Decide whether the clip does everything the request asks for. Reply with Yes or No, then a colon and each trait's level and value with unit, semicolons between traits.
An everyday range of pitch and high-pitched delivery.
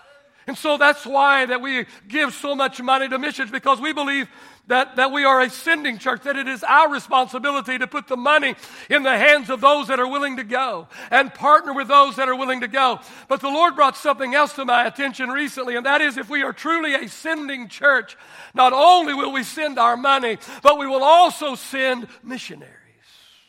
No: narrow, 1.9 semitones; very high, 270 Hz